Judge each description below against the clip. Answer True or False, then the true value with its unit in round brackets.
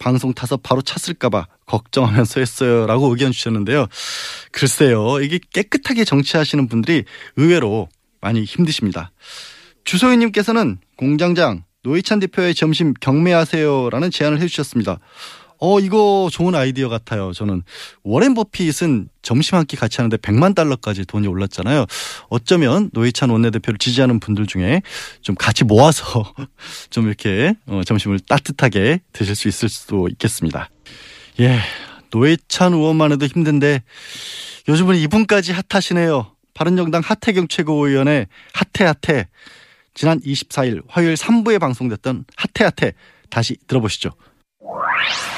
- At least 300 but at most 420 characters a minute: True (315 characters per minute)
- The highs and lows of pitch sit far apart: True (6.9 semitones)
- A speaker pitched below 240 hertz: True (135 Hz)